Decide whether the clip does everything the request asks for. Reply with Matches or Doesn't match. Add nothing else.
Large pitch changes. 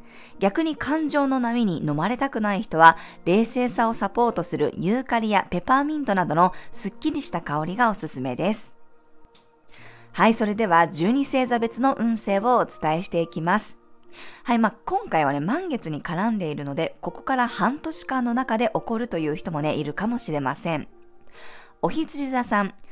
Matches